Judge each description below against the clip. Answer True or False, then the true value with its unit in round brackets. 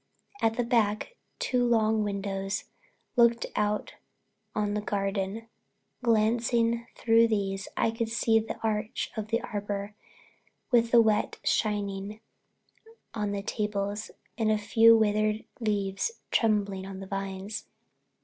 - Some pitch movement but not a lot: False (2.0 semitones)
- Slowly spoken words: True (125 wpm)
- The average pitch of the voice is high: True (215 Hz)